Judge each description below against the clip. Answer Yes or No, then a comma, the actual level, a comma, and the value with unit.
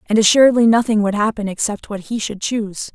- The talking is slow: No, fast, 205 wpm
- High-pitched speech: Yes, high, 215 Hz